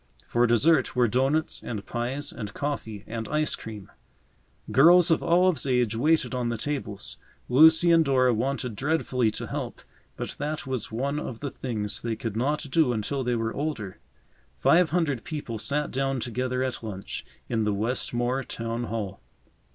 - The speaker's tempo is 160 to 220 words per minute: Yes, average, 165 wpm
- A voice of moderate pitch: No, low, 125 Hz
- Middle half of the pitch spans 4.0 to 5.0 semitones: Yes, average, 4.3 semitones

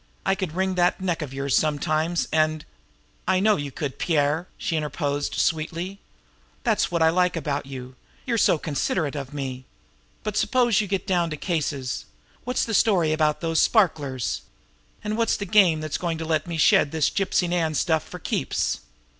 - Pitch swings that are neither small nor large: Yes, average, 3.8 semitones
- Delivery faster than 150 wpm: Yes, average, 180 wpm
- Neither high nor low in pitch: Yes, medium, 160 Hz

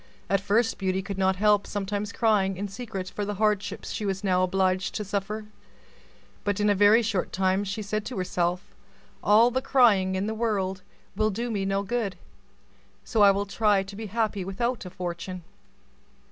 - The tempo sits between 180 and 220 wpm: Yes, average, 185 wpm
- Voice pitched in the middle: No, high, 200 Hz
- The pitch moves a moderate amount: No, narrow, 2.1 semitones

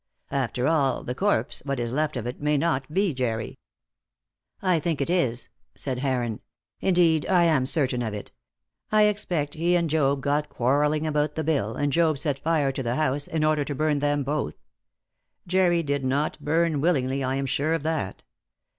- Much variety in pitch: No, average, 3.4 semitones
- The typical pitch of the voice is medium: Yes, medium, 145 Hz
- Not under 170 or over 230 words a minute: Yes, average, 185 wpm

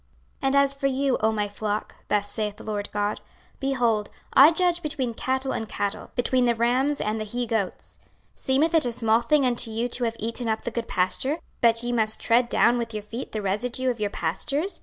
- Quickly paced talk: Yes, fast, 225 wpm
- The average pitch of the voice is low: No, high, 235 Hz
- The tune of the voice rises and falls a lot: No, average, 3.5 semitones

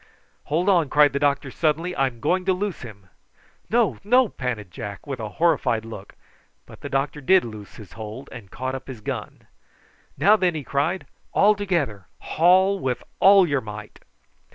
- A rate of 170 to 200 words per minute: Yes, average, 175 wpm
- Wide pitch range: Yes, wide, 8.0 semitones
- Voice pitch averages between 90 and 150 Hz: Yes, medium, 140 Hz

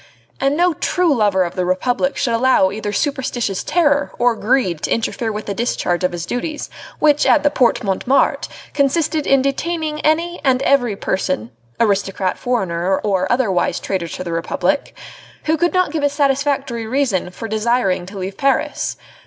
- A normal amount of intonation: No, wide, 6.8 semitones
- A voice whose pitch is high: Yes, high, 245 Hz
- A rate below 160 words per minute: No, average, 170 wpm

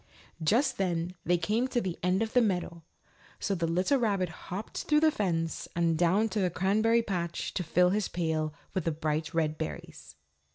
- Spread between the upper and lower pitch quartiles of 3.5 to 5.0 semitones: Yes, average, 4.3 semitones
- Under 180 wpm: No, average, 190 wpm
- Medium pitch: Yes, medium, 180 Hz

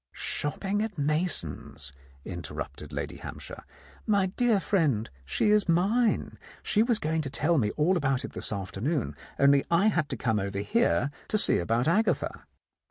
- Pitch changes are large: Yes, wide, 7.7 semitones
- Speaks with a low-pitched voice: No, medium, 160 Hz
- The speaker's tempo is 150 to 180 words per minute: Yes, average, 160 wpm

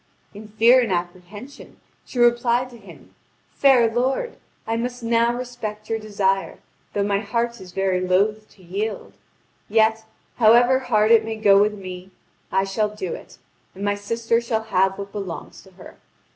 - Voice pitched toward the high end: Yes, high, 215 Hz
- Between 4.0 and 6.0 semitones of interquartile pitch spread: No, average, 3.0 semitones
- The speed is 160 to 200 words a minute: Yes, average, 165 wpm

